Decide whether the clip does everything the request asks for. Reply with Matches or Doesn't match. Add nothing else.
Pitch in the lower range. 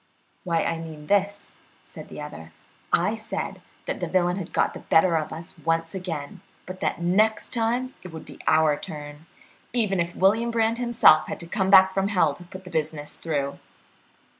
Doesn't match